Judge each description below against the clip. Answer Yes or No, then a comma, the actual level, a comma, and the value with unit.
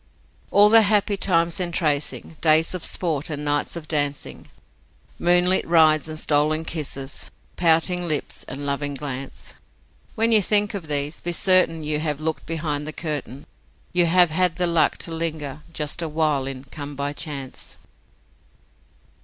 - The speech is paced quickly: No, average, 155 wpm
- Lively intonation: No, average, 3.0 semitones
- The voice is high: No, medium, 155 Hz